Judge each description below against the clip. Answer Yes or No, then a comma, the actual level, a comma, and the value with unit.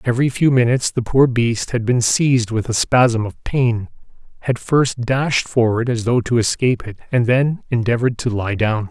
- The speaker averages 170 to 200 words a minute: Yes, average, 195 wpm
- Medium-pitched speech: No, low, 120 Hz